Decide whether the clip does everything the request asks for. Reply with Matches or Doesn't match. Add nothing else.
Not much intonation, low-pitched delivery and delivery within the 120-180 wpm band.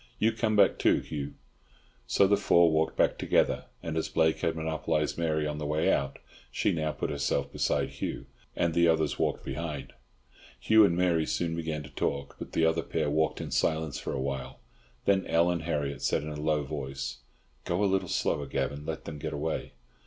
Doesn't match